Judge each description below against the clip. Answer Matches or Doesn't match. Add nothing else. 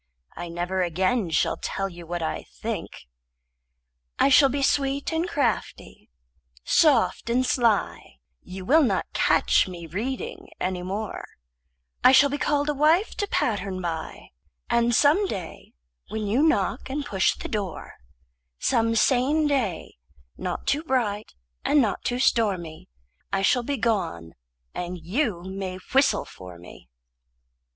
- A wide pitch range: Matches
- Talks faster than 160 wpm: Doesn't match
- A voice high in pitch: Matches